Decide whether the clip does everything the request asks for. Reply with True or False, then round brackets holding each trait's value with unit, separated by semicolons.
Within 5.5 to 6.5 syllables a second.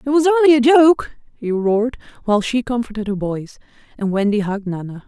True (5.8 syllables/s)